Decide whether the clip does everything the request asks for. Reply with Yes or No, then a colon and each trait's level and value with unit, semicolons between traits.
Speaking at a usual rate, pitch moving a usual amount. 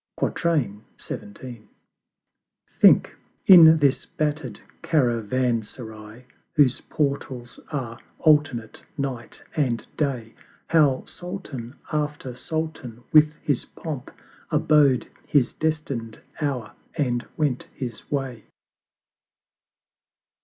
No: slow, 80 wpm; average, 4.1 semitones